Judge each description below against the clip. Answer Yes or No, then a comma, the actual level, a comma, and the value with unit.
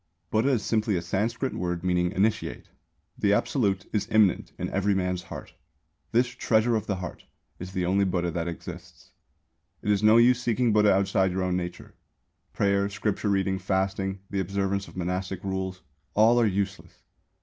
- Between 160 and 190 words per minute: Yes, average, 170 wpm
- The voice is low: Yes, low, 100 Hz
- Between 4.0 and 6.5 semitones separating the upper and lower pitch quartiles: No, narrow, 2.6 semitones